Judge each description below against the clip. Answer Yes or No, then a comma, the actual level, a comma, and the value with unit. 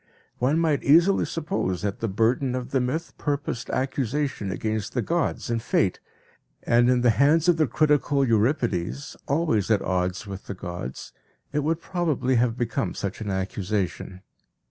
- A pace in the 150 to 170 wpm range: Yes, average, 160 wpm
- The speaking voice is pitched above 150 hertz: No, low, 125 Hz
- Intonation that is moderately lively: No, wide, 6.1 semitones